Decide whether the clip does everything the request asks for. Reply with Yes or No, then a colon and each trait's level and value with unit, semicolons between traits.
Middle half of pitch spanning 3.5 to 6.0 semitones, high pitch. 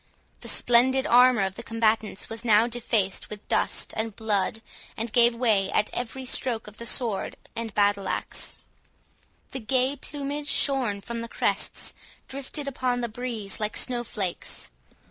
No: average, 2.9 semitones; high, 230 Hz